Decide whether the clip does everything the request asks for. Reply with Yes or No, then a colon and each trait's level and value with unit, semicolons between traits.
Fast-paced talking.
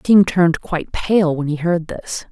Yes: fast, 235 wpm